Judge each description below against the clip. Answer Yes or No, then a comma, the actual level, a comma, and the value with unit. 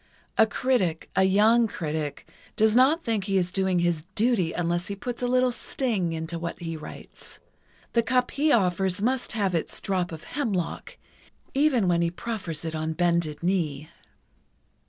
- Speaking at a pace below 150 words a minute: No, average, 155 wpm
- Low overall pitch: No, high, 190 Hz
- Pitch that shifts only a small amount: No, wide, 5.6 semitones